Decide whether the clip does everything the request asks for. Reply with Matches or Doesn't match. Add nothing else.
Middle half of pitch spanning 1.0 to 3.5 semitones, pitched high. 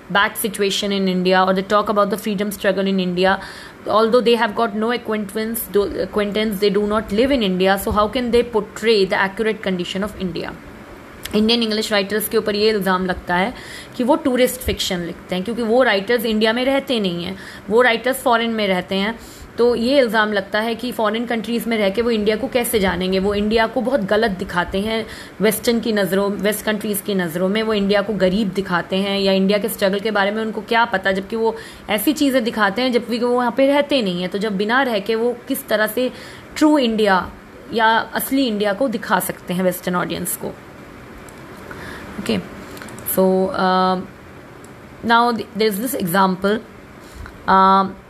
Matches